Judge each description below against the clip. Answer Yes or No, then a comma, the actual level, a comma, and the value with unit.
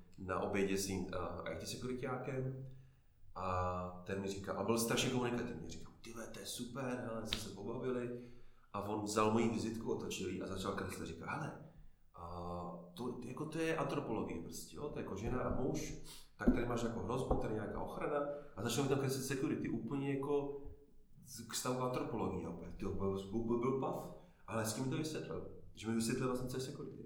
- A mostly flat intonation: No, average, 4.7 semitones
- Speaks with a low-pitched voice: Yes, low, 115 Hz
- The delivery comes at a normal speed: No, fast, 195 wpm